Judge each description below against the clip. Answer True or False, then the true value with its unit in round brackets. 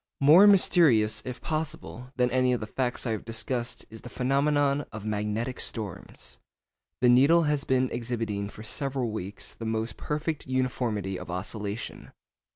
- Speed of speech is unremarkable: True (155 wpm)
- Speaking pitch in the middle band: False (125 Hz)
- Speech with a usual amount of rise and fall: True (4.1 semitones)